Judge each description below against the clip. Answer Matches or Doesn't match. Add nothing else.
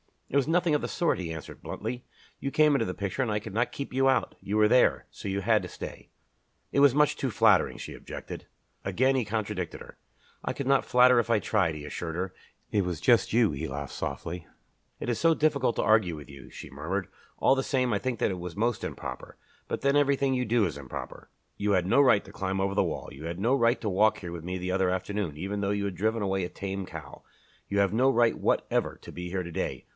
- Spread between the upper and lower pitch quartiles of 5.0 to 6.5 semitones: Matches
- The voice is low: Matches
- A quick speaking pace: Matches